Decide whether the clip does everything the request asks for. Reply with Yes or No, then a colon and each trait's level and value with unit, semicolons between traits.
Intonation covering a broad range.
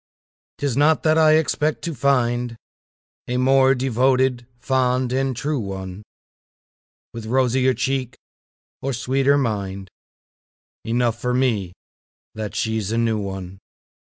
No: average, 3.2 semitones